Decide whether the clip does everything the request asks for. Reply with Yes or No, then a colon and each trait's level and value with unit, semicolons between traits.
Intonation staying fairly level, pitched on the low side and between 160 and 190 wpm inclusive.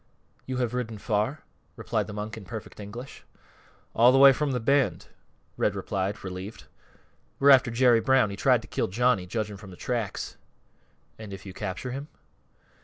No: average, 3.9 semitones; low, 115 Hz; average, 175 wpm